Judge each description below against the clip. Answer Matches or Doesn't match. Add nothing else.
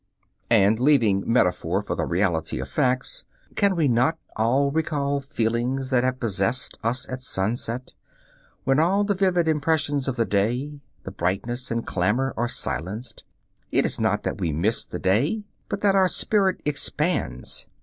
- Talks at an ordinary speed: Matches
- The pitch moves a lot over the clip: Matches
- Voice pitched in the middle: Doesn't match